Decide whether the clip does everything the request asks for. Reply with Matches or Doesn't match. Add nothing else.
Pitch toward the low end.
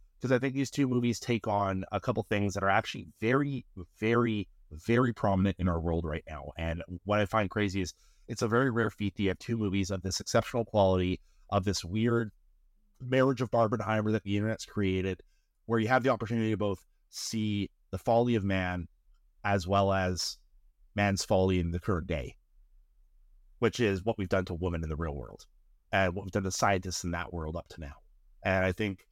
Matches